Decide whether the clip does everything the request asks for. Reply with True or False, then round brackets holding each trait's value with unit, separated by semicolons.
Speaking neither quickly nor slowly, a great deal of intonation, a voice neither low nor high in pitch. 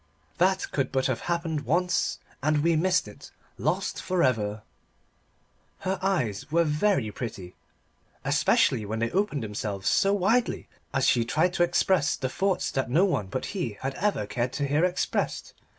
True (165 wpm; 7.5 semitones; 150 Hz)